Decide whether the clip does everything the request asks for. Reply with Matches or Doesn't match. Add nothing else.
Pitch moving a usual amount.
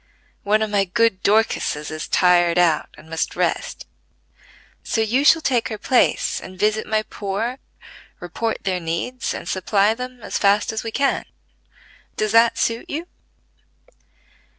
Matches